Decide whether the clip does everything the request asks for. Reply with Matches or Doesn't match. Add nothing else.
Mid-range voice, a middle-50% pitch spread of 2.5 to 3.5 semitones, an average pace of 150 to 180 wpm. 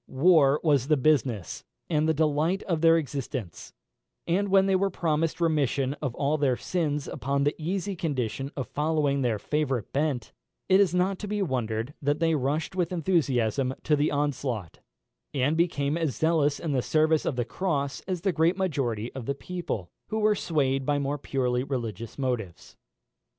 Doesn't match